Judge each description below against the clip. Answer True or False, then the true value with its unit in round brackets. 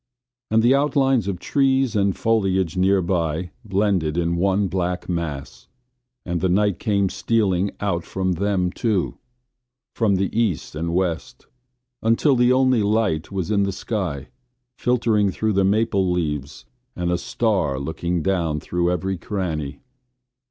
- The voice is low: True (95 Hz)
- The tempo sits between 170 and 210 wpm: False (145 wpm)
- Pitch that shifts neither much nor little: True (3.7 semitones)